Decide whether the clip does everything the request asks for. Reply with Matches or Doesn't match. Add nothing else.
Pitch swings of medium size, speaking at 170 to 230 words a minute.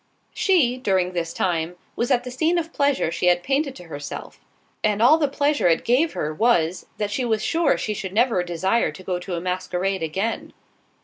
Doesn't match